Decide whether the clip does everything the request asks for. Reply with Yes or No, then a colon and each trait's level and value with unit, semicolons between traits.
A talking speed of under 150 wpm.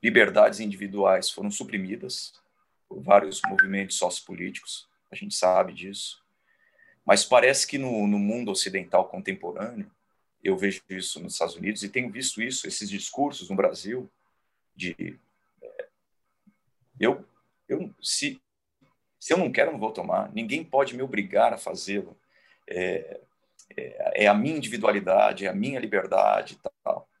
Yes: average, 140 wpm